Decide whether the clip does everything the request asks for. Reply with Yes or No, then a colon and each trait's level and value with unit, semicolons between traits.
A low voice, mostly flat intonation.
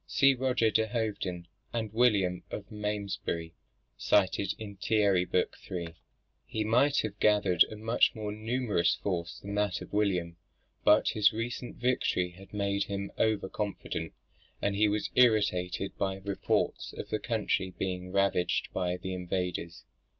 No: low, 100 Hz; average, 3.0 semitones